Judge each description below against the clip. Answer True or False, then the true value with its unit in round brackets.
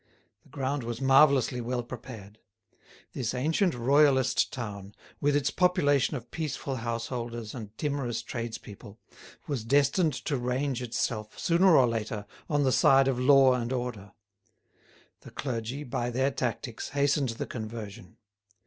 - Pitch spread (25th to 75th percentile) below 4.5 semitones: True (3.3 semitones)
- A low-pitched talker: True (125 Hz)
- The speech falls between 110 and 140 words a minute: True (135 wpm)